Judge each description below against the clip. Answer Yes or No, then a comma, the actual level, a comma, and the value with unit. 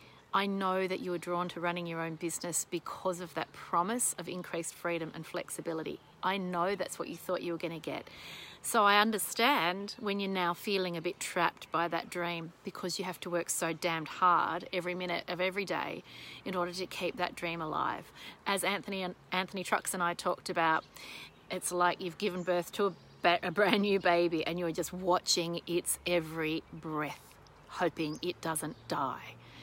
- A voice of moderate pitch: Yes, medium, 175 Hz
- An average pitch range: No, narrow, 1.6 semitones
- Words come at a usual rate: Yes, average, 190 wpm